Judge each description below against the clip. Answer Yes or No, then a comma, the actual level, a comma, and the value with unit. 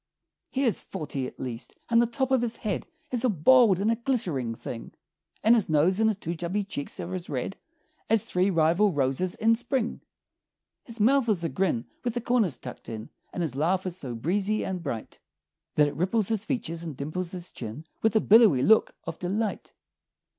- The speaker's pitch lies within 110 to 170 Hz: No, medium, 185 Hz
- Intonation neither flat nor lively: No, wide, 6.4 semitones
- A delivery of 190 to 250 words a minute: Yes, average, 200 wpm